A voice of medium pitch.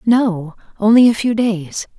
No: high, 210 Hz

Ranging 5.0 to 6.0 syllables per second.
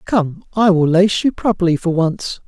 No: 4.5 syllables/s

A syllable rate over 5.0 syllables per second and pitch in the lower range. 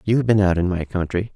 Yes: 6.4 syllables/s; very low, 95 Hz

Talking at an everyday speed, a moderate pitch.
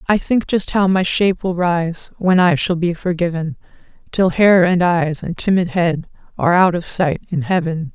Yes: average, 195 wpm; medium, 180 Hz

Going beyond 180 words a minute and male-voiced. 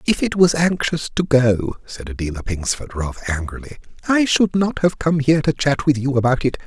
Yes: fast, 205 wpm; male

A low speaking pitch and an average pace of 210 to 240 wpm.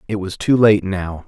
Yes: low, 100 Hz; fast, 235 wpm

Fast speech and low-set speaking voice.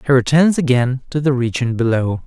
No: average, 185 wpm; low, 130 Hz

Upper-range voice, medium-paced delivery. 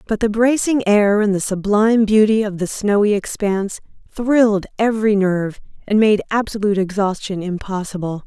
Yes: high, 205 Hz; average, 145 wpm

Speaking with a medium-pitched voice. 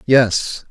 No: low, 120 Hz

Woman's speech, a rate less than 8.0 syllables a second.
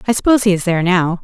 No: female; 8.6 syllables/s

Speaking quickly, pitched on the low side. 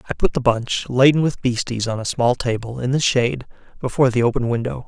Yes: fast, 220 wpm; low, 125 Hz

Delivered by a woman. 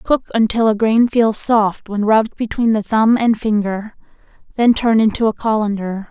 Yes: female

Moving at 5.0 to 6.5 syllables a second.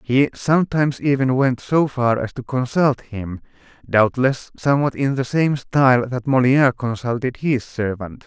No: 4.6 syllables/s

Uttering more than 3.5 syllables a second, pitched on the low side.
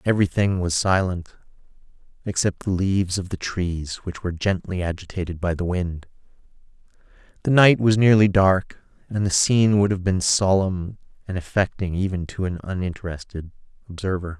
Yes: 5.2 syllables/s; very low, 95 Hz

